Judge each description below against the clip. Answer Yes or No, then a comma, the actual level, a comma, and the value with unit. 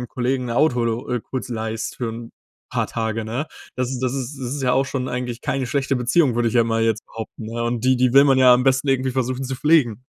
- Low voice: Yes, low, 125 Hz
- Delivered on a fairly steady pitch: Yes, narrow, 2.1 semitones